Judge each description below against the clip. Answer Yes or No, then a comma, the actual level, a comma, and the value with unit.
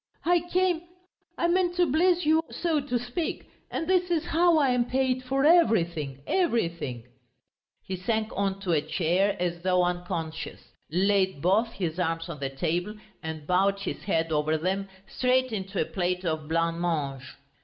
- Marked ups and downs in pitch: Yes, wide, 8.1 semitones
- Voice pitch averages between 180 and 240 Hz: Yes, high, 190 Hz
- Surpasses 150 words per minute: Yes, average, 165 wpm